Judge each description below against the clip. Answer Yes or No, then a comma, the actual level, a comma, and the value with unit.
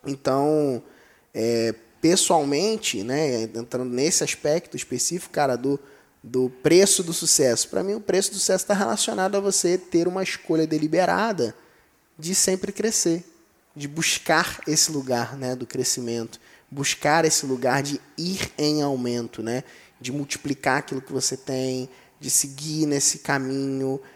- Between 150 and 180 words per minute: No, average, 140 wpm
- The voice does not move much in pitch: No, average, 5.2 semitones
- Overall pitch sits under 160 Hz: Yes, medium, 140 Hz